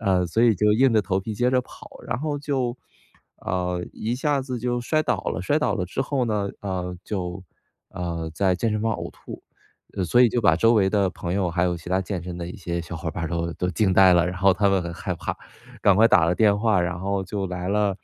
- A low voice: Yes, very low, 95 Hz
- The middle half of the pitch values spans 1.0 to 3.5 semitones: No, average, 4.0 semitones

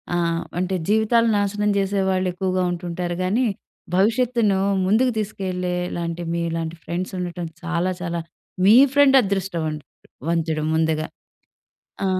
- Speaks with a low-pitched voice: No, medium, 185 Hz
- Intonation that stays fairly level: No, average, 3.1 semitones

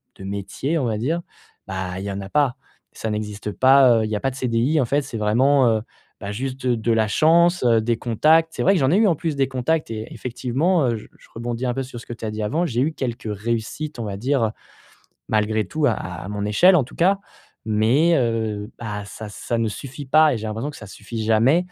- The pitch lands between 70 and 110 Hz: No, low, 120 Hz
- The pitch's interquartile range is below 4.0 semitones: No, average, 4.7 semitones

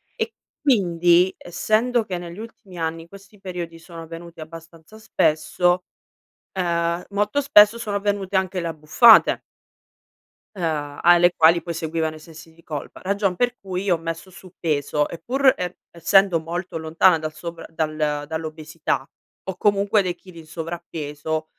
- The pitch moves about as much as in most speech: Yes, average, 3.2 semitones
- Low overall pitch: No, medium, 170 Hz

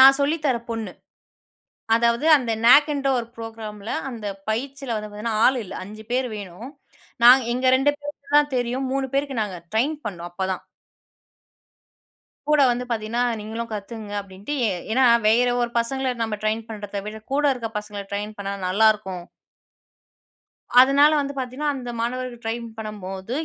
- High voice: Yes, high, 230 Hz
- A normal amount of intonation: Yes, average, 3.8 semitones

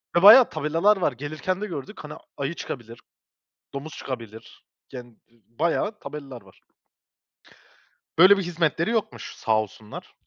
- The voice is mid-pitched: Yes, medium, 150 Hz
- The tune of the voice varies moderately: No, wide, 7.4 semitones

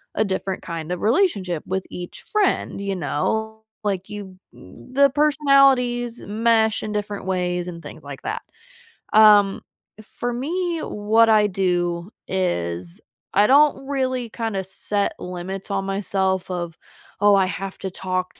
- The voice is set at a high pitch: Yes, high, 200 Hz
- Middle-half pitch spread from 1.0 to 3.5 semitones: No, average, 4.0 semitones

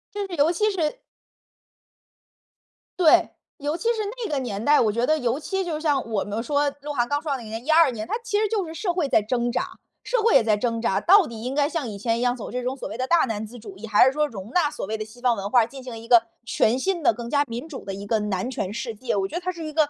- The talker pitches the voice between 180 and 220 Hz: No, very high, 255 Hz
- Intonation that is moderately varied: No, wide, 5.7 semitones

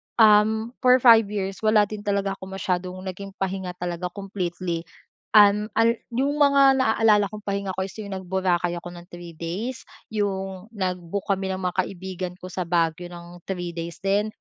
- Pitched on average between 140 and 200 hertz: Yes, high, 190 Hz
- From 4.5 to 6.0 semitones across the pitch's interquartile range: No, average, 2.8 semitones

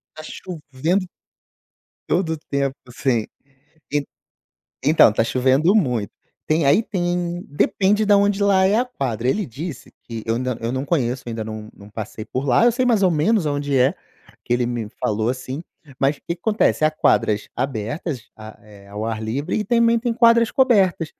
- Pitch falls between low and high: Yes, medium, 145 Hz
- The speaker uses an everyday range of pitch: No, wide, 8.0 semitones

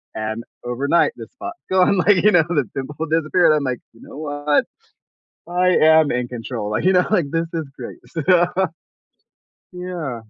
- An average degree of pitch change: No, wide, 5.7 semitones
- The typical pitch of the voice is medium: Yes, medium, 155 Hz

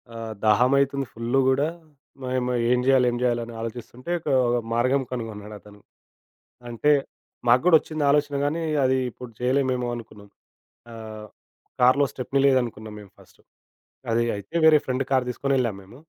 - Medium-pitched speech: No, low, 125 Hz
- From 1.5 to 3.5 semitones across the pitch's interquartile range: Yes, average, 2.9 semitones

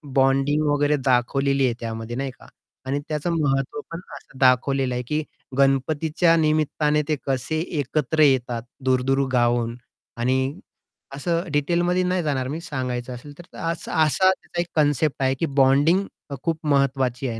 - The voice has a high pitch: No, medium, 140 Hz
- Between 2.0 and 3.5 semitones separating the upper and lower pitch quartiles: Yes, average, 3.2 semitones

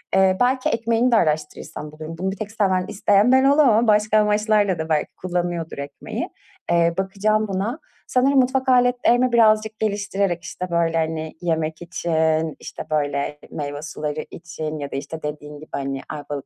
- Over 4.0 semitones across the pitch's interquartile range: Yes, wide, 5.6 semitones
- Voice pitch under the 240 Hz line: Yes, medium, 185 Hz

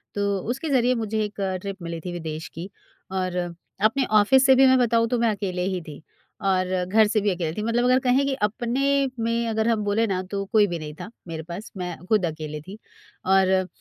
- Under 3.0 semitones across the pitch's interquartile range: No, average, 4.1 semitones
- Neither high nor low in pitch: No, high, 205 Hz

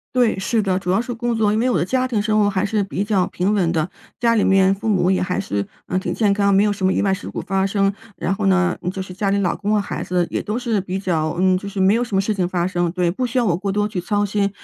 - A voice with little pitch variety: Yes, narrow, 2.2 semitones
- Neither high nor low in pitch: No, high, 195 Hz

